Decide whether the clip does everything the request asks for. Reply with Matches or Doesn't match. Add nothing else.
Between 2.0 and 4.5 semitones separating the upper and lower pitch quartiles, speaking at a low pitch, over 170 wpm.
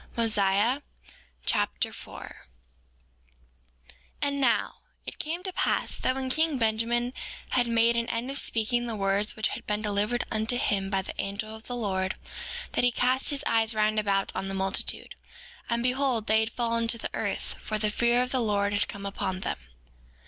Doesn't match